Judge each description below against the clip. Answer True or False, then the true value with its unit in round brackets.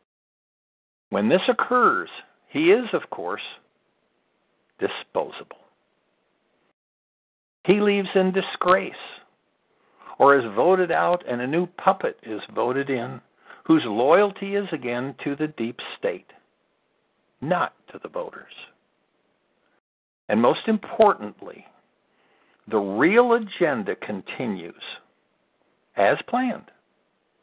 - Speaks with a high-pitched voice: True (200 Hz)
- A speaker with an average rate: False (95 wpm)